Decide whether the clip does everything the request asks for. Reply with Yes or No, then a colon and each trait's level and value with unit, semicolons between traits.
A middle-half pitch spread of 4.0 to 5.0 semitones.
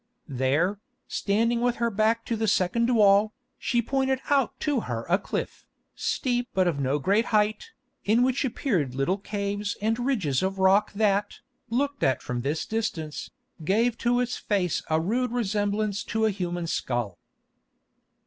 Yes: average, 4.6 semitones